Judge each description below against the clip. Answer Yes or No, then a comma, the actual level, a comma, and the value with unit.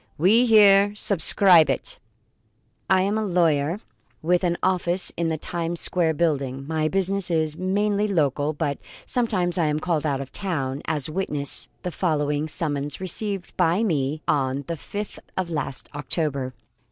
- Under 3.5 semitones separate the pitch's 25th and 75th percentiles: No, average, 4.3 semitones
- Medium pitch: Yes, medium, 165 Hz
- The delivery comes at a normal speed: Yes, average, 155 wpm